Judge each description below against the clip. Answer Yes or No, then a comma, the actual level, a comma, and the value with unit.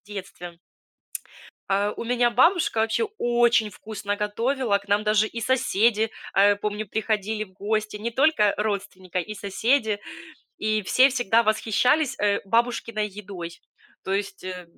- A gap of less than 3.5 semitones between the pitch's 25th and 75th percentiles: Yes, narrow, 2.6 semitones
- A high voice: Yes, high, 215 Hz